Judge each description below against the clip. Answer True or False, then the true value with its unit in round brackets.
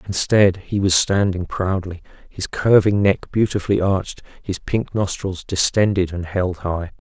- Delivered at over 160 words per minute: False (145 wpm)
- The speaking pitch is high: False (95 Hz)